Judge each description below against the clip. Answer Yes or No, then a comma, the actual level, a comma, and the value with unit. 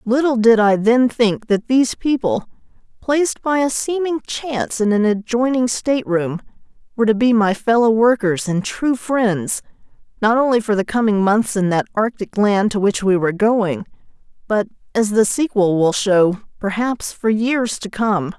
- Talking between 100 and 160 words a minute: No, average, 170 wpm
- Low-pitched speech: No, high, 220 Hz